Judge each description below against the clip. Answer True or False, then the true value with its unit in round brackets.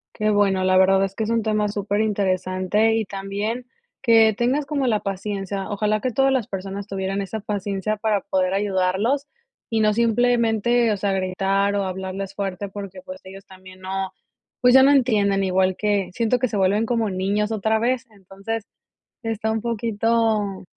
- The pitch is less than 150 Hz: False (205 Hz)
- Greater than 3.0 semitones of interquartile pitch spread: False (2.6 semitones)